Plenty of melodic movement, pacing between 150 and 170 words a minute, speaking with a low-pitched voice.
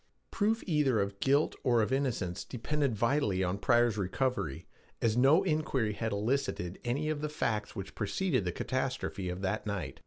Yes: wide, 5.7 semitones; average, 165 wpm; low, 120 Hz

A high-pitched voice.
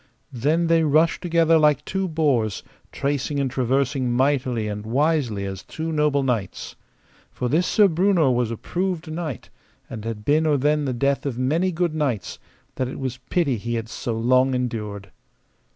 No: medium, 140 Hz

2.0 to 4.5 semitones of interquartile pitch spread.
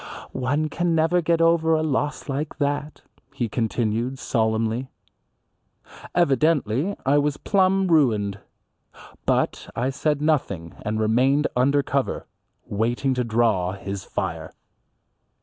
No: wide, 5.5 semitones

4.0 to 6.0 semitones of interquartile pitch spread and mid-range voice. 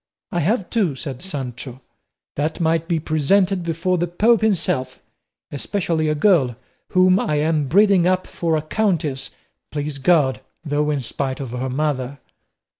Yes: average, 4.7 semitones; medium, 155 Hz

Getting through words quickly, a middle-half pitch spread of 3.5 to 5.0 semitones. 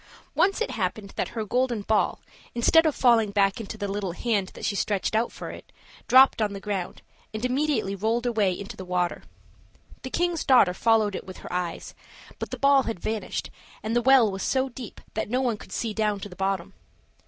Yes: fast, 210 wpm; average, 3.9 semitones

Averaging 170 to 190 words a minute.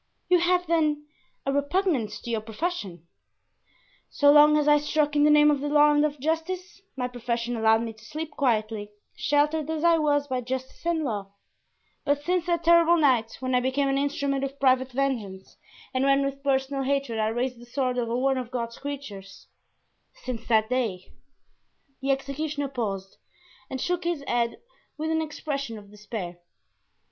Yes: average, 175 wpm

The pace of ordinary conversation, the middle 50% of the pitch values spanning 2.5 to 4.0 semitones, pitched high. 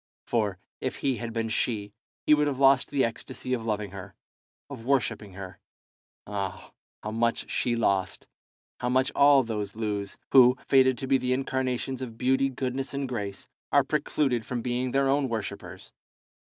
No: average, 165 wpm; average, 3.6 semitones; low, 125 Hz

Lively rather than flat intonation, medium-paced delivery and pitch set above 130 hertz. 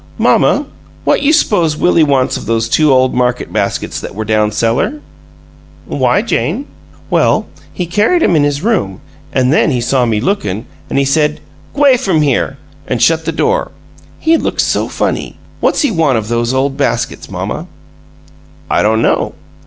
Yes: wide, 6.8 semitones; average, 170 wpm; medium, 140 Hz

